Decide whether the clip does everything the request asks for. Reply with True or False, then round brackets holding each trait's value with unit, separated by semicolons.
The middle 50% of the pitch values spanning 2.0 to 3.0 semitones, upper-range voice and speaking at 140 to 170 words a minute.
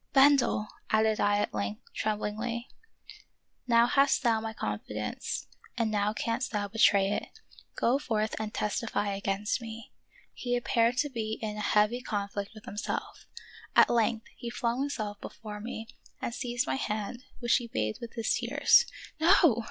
True (2.5 semitones; 220 Hz; 160 wpm)